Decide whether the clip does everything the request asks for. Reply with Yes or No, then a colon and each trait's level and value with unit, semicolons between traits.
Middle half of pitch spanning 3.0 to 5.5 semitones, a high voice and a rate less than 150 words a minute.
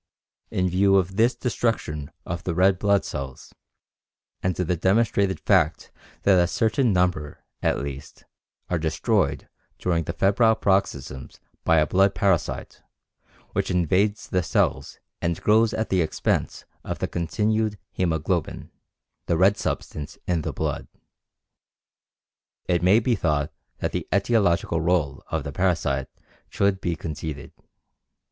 No: average, 3.7 semitones; very low, 90 Hz; slow, 135 wpm